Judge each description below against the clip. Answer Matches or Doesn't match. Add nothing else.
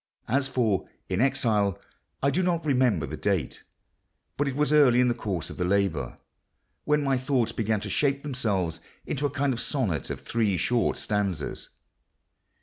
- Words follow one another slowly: Doesn't match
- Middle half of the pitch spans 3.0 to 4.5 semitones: Doesn't match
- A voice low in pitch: Matches